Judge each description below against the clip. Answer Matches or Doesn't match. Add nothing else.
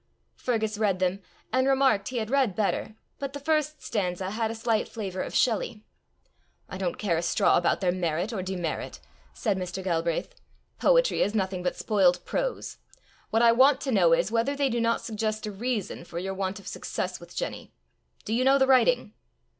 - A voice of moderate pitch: Doesn't match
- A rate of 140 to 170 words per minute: Doesn't match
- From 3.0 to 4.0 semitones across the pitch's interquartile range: Doesn't match